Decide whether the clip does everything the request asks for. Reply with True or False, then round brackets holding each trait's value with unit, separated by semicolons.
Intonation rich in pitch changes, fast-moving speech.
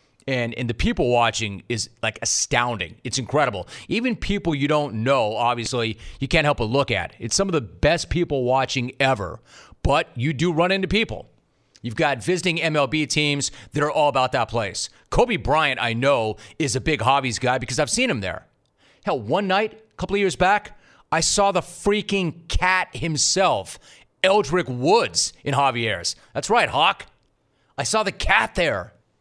False (6.3 semitones; 180 wpm)